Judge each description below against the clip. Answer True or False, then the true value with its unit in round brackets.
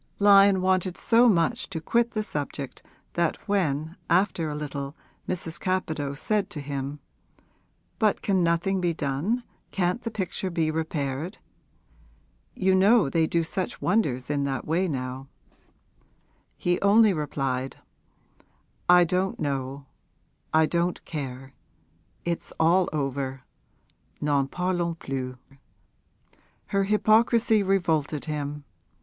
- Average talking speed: False (120 wpm)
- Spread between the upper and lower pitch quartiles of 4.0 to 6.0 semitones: True (5.1 semitones)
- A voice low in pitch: False (170 Hz)